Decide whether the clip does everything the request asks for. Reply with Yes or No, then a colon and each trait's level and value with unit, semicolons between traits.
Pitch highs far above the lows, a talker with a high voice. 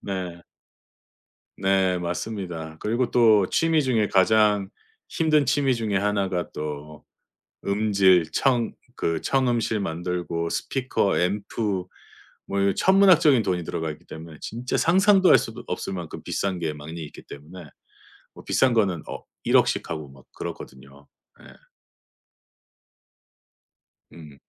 No: wide, 5.8 semitones; very low, 95 Hz